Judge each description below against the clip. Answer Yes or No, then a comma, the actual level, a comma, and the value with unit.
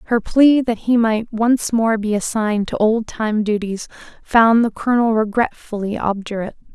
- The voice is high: Yes, high, 220 Hz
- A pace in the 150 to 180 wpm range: Yes, average, 160 wpm